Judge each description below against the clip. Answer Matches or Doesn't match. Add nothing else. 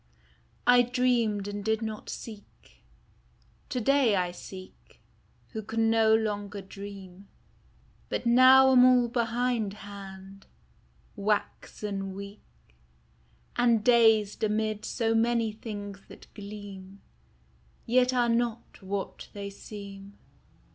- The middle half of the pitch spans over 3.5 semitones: Doesn't match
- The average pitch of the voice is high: Matches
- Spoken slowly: Matches